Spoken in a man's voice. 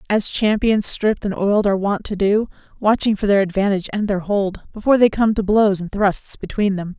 No: female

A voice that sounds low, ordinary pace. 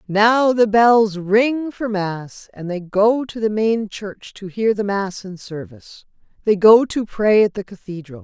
No: high, 205 Hz; average, 190 wpm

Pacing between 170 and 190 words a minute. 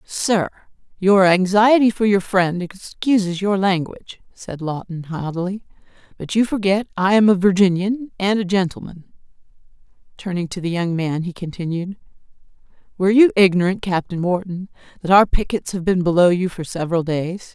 No: average, 150 wpm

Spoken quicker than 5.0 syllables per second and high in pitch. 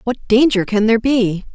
Yes: 5.5 syllables/s; high, 225 Hz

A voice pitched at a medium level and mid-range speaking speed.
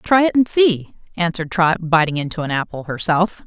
Yes: medium, 175 Hz; average, 190 wpm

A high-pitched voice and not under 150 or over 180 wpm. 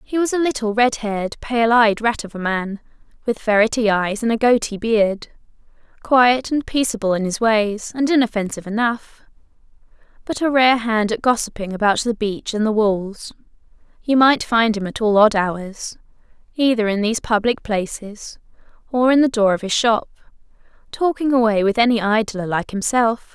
Yes: high, 225 Hz; average, 170 wpm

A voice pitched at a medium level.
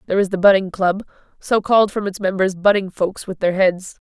No: high, 195 Hz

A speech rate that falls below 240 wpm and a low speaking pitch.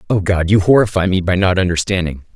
Yes: fast, 205 wpm; very low, 95 Hz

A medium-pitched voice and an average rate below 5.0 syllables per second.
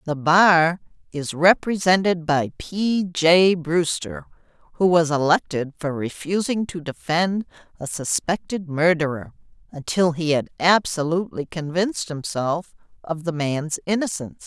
Yes: medium, 170 Hz; 4.2 syllables/s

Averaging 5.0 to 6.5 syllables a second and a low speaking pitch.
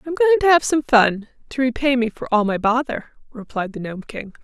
No: 5.1 syllables/s; very high, 250 Hz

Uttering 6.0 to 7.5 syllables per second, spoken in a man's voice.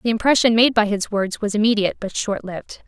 No: 6.1 syllables/s; female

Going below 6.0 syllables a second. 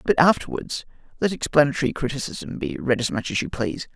No: 6.1 syllables/s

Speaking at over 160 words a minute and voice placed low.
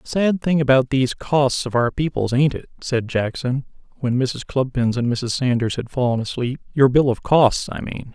Yes: average, 200 wpm; low, 130 Hz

